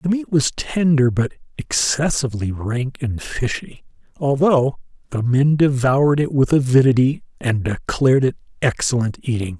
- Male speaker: Yes, male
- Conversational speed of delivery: No, slow, 130 wpm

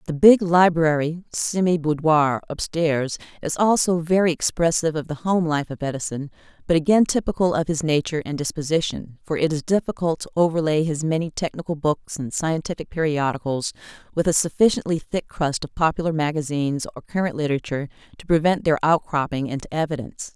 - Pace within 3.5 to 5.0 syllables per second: No, 5.8 syllables/s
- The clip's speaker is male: No, female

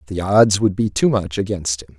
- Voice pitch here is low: Yes, very low, 95 Hz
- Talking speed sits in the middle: No, fast, 240 wpm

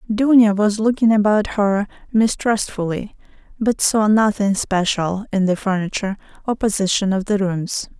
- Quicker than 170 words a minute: No, slow, 135 wpm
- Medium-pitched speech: No, high, 205 Hz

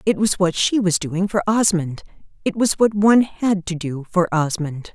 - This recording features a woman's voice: Yes, female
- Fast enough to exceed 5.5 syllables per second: No, 4.7 syllables/s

